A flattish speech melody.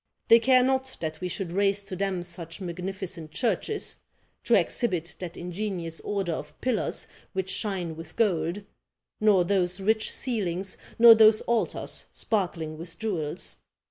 No: average, 4.0 semitones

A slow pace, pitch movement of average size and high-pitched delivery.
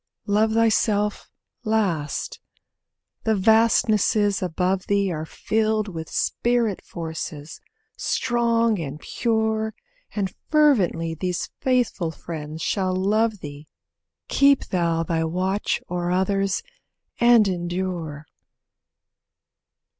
Yes: slow, 95 wpm; average, 4.5 semitones; high, 195 Hz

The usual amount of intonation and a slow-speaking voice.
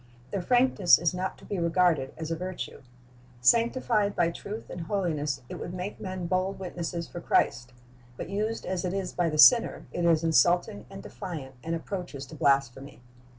No: average, 3.3 semitones; average, 180 wpm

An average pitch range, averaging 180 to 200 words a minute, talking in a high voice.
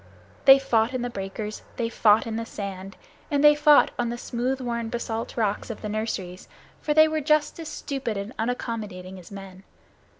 Yes: average, 4.5 semitones; average, 190 wpm; high, 230 Hz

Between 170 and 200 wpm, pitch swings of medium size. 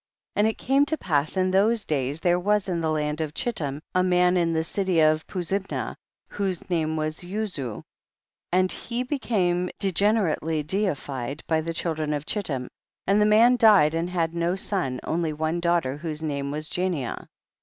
Yes: average, 180 wpm; average, 4.0 semitones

